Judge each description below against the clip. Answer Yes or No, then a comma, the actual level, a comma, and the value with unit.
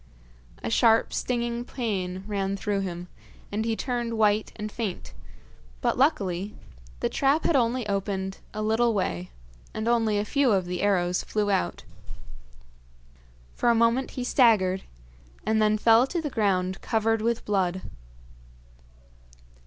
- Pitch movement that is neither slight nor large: Yes, average, 3.4 semitones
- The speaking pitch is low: No, high, 215 Hz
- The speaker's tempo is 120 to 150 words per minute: Yes, average, 140 wpm